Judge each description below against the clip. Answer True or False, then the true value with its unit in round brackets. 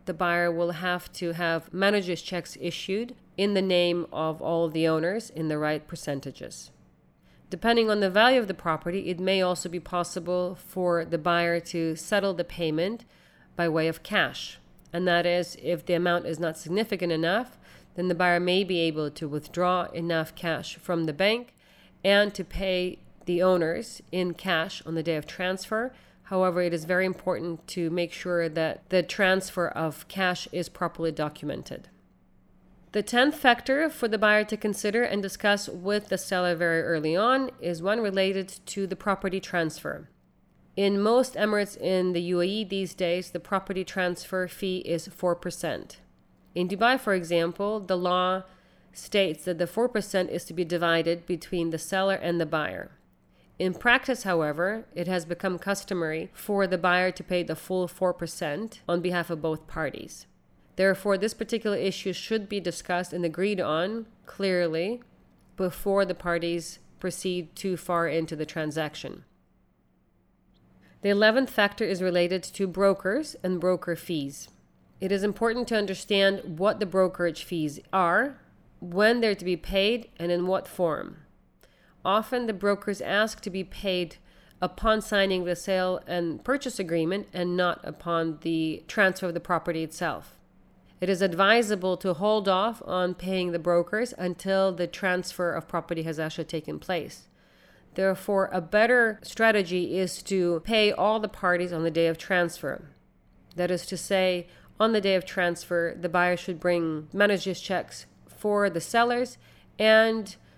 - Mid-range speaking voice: True (180 Hz)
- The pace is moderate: True (160 wpm)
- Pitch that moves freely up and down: False (2.6 semitones)